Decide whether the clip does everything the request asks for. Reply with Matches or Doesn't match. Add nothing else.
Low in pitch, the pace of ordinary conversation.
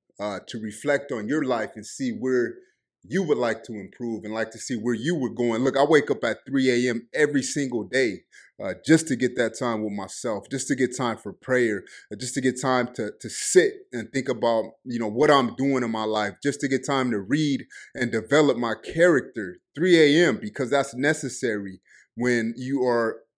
Doesn't match